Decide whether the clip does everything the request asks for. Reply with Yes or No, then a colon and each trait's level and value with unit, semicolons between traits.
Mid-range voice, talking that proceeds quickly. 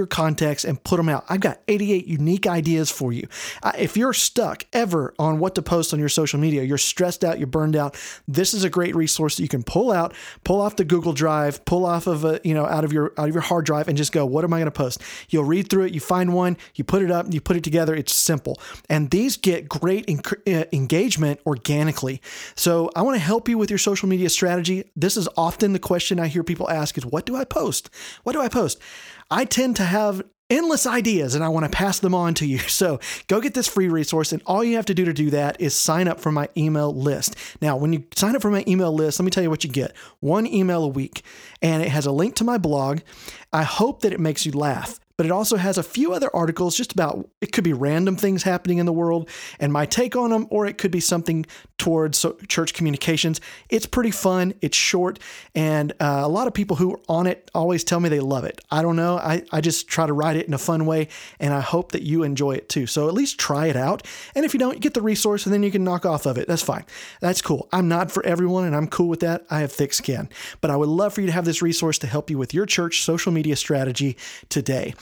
Yes: medium, 170 Hz; fast, 260 wpm